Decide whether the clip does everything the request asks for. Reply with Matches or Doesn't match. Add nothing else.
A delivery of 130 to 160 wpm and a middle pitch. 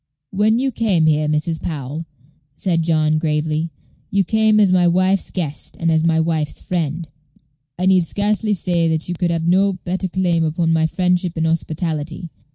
Doesn't match